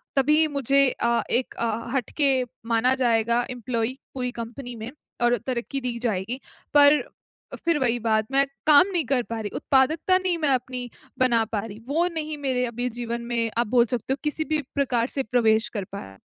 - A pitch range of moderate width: Yes, average, 3.1 semitones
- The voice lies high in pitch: Yes, very high, 250 Hz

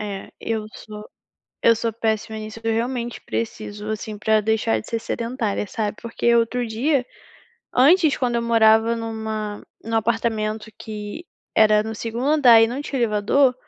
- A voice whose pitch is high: Yes, high, 225 Hz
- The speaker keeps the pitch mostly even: Yes, narrow, 1.6 semitones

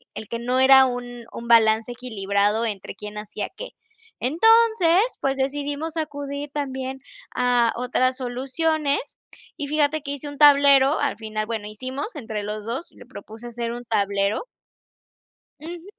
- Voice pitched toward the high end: Yes, very high, 255 Hz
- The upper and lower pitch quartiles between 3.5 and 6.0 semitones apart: Yes, average, 4.2 semitones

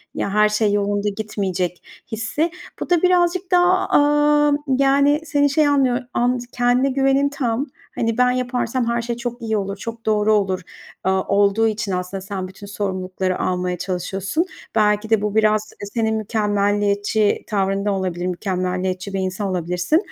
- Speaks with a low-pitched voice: No, high, 215 Hz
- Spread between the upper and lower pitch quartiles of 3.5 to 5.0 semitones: Yes, average, 4.4 semitones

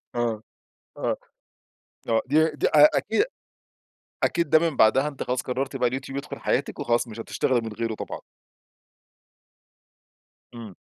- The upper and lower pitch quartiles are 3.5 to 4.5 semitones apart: Yes, average, 4.2 semitones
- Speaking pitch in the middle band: No, low, 130 Hz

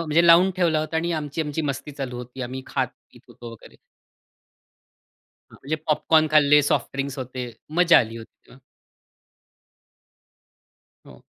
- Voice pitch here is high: No, medium, 145 Hz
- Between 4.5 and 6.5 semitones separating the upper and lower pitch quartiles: No, average, 3.5 semitones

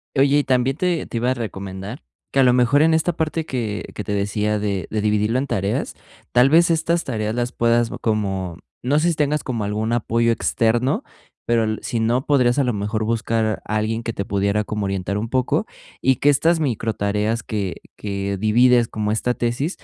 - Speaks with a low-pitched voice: Yes, low, 115 Hz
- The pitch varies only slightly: No, average, 3.9 semitones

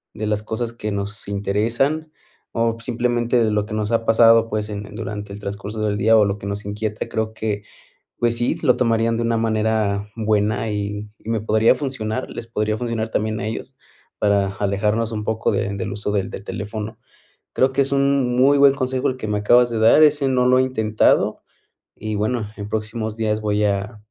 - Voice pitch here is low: Yes, low, 110 Hz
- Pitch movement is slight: Yes, narrow, 2.1 semitones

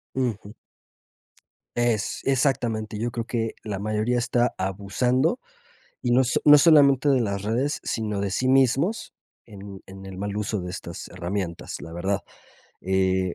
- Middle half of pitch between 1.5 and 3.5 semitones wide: No, average, 4.5 semitones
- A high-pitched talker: No, low, 110 Hz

